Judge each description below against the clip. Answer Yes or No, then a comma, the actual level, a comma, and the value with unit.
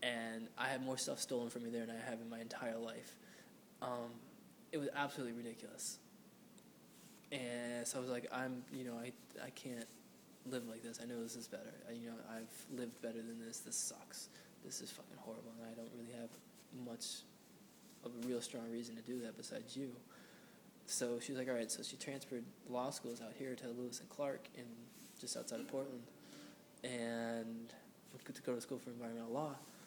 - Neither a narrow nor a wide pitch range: No, narrow, 1.8 semitones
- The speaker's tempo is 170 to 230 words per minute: Yes, fast, 205 wpm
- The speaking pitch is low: Yes, low, 120 Hz